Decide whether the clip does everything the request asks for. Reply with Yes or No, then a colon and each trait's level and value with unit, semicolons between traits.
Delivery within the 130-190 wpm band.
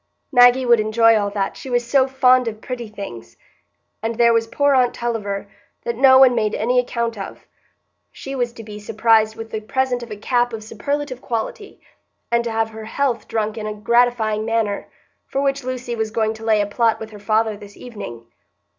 No: average, 200 wpm